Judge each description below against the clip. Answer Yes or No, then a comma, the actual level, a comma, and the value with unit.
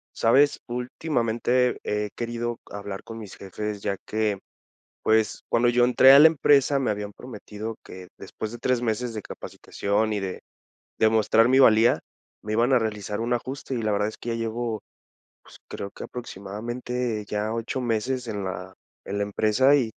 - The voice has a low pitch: Yes, low, 115 Hz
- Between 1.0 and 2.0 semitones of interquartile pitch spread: No, average, 2.7 semitones